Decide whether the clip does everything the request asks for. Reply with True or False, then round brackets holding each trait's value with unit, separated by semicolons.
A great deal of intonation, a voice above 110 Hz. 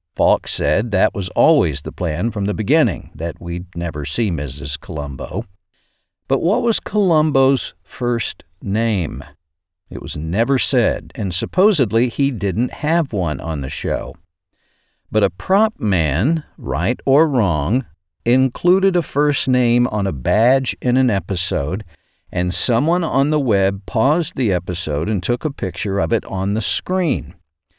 False (7.5 semitones; 105 Hz)